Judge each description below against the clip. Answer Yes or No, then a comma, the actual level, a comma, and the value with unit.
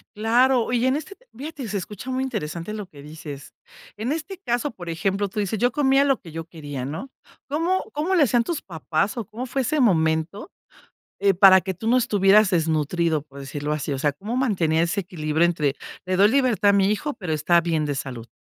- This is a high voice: Yes, high, 195 Hz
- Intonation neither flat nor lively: No, wide, 7.7 semitones